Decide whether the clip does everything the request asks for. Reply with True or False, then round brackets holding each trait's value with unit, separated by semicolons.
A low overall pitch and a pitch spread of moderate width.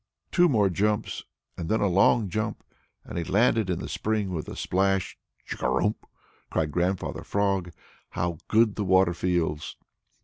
True (95 Hz; 3.4 semitones)